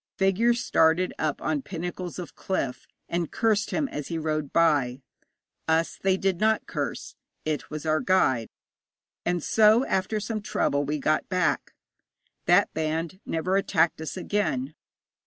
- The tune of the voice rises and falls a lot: No, average, 3.8 semitones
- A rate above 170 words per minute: No, average, 145 wpm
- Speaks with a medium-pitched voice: Yes, medium, 170 Hz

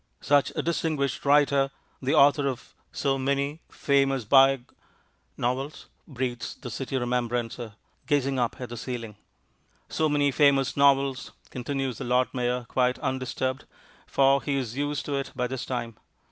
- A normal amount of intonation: No, narrow, 2.1 semitones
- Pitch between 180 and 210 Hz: No, low, 135 Hz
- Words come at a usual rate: Yes, average, 150 wpm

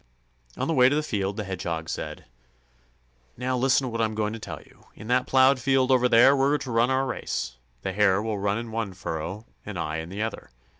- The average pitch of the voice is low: Yes, low, 115 Hz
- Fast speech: Yes, fast, 230 wpm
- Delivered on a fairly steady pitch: No, average, 4.8 semitones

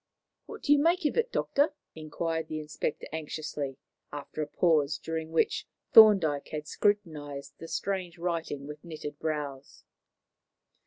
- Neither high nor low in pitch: Yes, medium, 160 Hz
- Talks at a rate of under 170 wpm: Yes, average, 140 wpm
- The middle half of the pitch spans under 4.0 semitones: Yes, average, 3.5 semitones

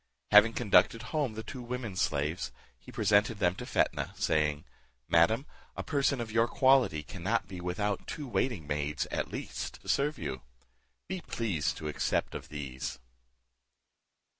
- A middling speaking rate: Yes, average, 150 wpm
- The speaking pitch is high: No, low, 105 Hz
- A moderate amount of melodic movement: No, wide, 7.5 semitones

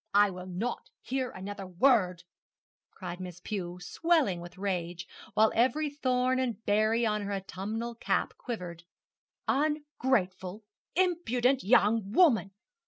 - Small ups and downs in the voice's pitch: No, wide, 5.5 semitones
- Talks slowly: Yes, slow, 120 wpm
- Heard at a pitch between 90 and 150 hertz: No, high, 215 Hz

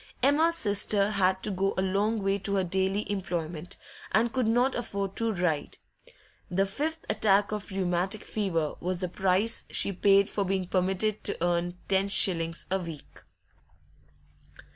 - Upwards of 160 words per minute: No, average, 155 wpm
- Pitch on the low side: No, high, 195 Hz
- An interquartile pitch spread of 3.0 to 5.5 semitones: No, narrow, 2.5 semitones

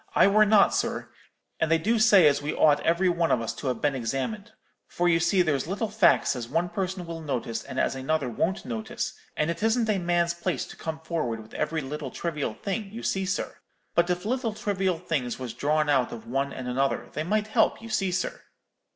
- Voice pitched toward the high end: No, medium, 165 Hz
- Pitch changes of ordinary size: No, wide, 5.8 semitones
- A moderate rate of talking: No, fast, 220 wpm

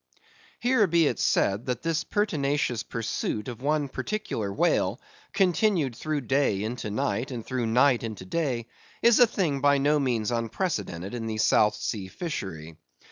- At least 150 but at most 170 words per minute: Yes, average, 155 wpm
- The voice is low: Yes, low, 130 Hz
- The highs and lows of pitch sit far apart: Yes, wide, 6.0 semitones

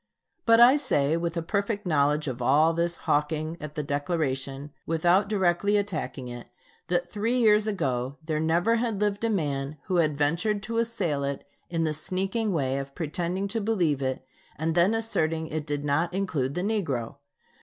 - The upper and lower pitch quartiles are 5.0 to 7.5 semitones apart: Yes, wide, 5.6 semitones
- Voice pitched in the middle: Yes, medium, 165 Hz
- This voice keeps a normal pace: Yes, average, 175 wpm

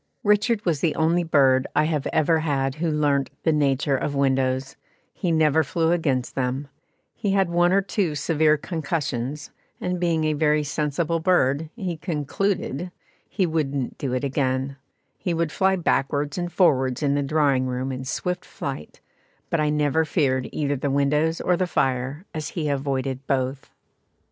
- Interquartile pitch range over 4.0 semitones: No, average, 3.5 semitones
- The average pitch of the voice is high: No, medium, 150 Hz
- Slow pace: No, average, 165 wpm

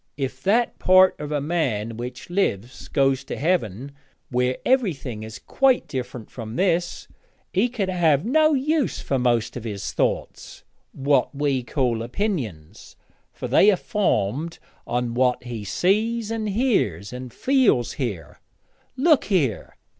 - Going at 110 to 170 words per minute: Yes, average, 140 wpm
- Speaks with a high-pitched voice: No, medium, 140 Hz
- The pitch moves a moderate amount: No, wide, 8.6 semitones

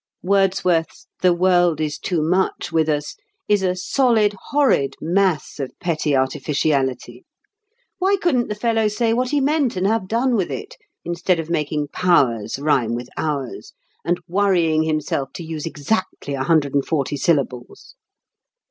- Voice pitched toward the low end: No, medium, 170 Hz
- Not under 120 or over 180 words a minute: Yes, average, 150 wpm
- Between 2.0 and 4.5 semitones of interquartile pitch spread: No, wide, 5.5 semitones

